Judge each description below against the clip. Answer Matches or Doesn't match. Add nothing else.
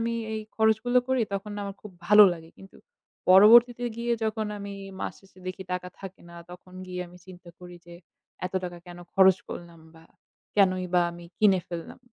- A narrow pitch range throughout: Doesn't match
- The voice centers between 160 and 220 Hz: Matches